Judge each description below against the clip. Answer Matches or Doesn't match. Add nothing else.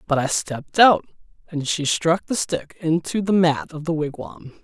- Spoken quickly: Doesn't match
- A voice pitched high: Doesn't match